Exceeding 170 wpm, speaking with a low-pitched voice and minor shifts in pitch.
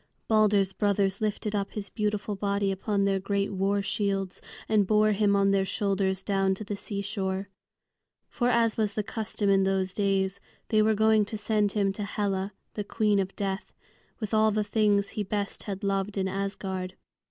No: average, 180 wpm; high, 200 Hz; narrow, 1.4 semitones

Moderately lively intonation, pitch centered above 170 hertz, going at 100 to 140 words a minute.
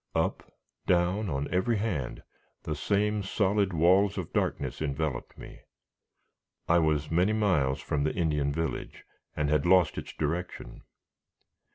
No: average, 4.6 semitones; very low, 85 Hz; slow, 135 wpm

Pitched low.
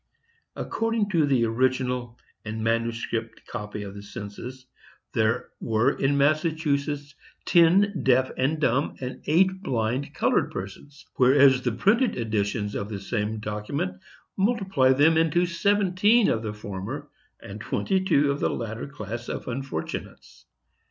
Yes: low, 130 Hz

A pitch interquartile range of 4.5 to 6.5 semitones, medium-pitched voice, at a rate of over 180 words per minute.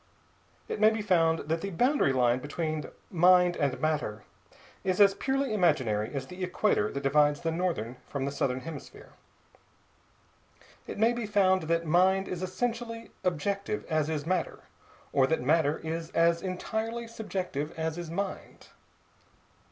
No: average, 5.0 semitones; medium, 170 Hz; average, 150 wpm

